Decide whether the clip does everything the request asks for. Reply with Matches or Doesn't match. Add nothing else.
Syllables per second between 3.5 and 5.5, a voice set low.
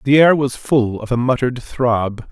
Matches